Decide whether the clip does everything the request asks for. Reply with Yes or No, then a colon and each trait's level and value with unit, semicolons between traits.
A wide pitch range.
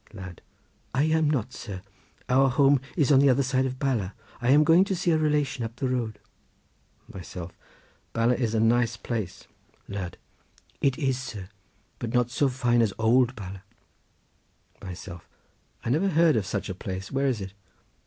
No: average, 4.6 semitones